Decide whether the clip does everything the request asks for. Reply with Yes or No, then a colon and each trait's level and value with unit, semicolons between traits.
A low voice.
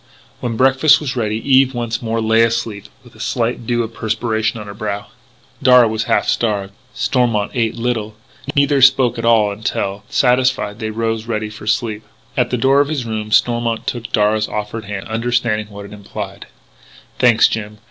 Yes: low, 115 Hz